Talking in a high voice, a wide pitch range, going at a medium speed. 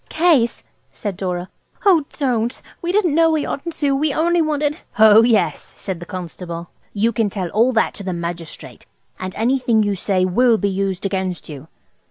Yes: high, 220 Hz; wide, 7.4 semitones; average, 180 wpm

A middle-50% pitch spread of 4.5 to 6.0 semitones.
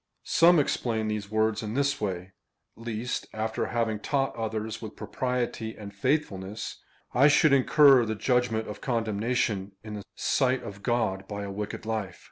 No: average, 3.2 semitones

